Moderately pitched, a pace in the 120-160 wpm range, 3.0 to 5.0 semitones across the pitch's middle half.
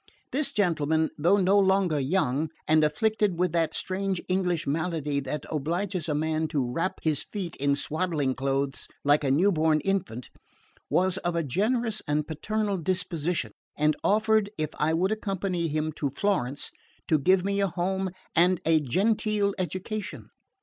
Yes: medium, 170 Hz; average, 155 wpm; average, 4.3 semitones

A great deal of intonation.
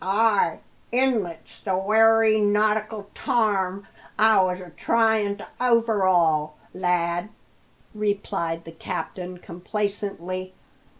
No: average, 3.3 semitones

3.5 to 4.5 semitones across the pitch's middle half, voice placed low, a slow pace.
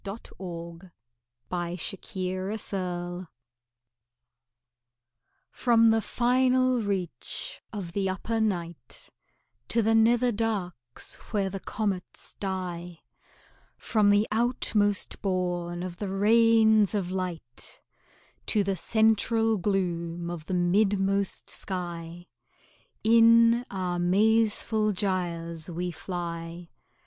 No: average, 3.8 semitones; high, 195 Hz; slow, 100 wpm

